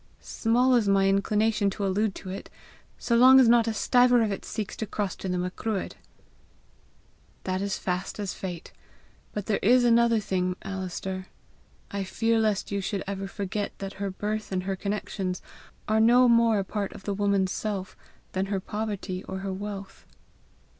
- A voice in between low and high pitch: No, high, 200 Hz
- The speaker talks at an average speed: Yes, average, 175 wpm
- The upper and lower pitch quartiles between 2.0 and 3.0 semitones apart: Yes, narrow, 2.4 semitones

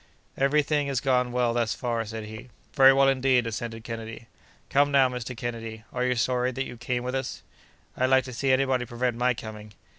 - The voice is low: Yes, low, 125 Hz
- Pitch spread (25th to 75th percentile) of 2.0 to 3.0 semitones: Yes, narrow, 2.4 semitones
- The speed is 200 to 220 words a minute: Yes, fast, 205 wpm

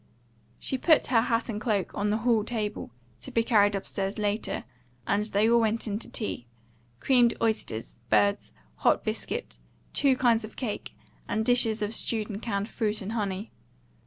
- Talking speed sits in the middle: Yes, average, 170 wpm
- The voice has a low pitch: No, high, 215 Hz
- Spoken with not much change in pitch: Yes, narrow, 2.3 semitones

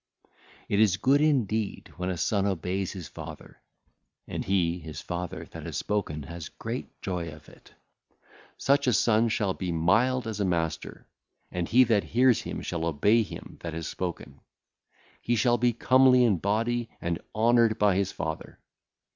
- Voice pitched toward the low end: Yes, low, 100 Hz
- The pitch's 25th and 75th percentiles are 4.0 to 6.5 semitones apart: Yes, average, 5.3 semitones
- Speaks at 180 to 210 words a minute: No, average, 165 wpm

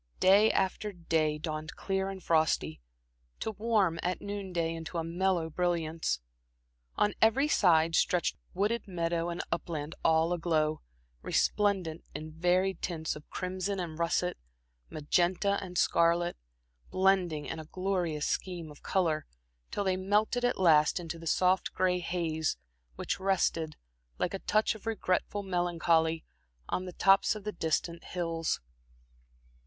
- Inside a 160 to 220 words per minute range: No, average, 140 wpm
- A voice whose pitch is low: No, medium, 175 Hz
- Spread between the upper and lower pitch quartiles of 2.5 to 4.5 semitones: Yes, average, 2.9 semitones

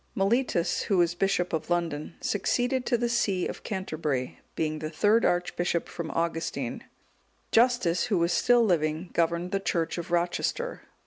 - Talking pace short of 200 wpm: Yes, average, 155 wpm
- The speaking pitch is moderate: Yes, medium, 175 Hz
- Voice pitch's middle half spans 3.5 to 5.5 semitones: Yes, average, 4.0 semitones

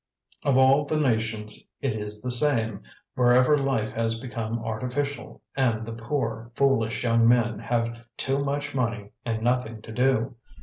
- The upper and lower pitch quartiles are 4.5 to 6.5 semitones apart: No, average, 2.9 semitones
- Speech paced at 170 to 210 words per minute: No, average, 155 wpm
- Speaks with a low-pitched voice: Yes, low, 115 Hz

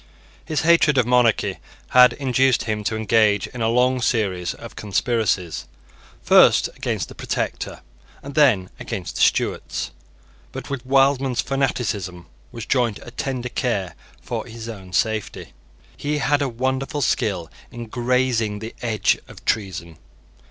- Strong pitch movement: No, average, 3.8 semitones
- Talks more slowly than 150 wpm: Yes, average, 140 wpm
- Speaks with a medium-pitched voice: No, low, 120 Hz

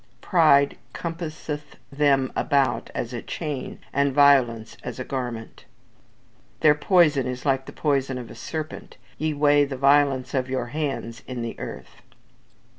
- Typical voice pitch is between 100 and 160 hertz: Yes, medium, 140 Hz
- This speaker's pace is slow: No, average, 145 wpm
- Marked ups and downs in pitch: No, narrow, 2.6 semitones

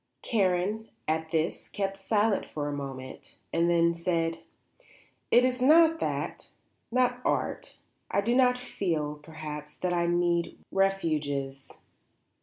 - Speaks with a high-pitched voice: No, medium, 175 Hz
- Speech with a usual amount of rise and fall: No, wide, 5.8 semitones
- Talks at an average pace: No, slow, 125 wpm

